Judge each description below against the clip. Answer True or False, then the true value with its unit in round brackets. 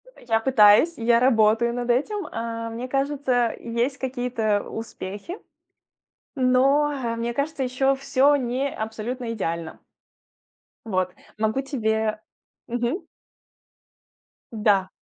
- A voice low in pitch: False (240 Hz)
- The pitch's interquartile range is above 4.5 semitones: False (3.3 semitones)